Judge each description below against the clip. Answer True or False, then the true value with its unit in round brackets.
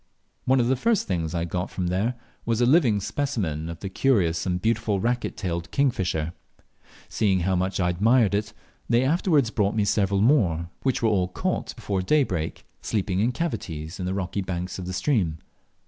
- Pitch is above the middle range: False (100 Hz)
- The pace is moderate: True (185 wpm)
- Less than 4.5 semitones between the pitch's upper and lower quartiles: False (4.9 semitones)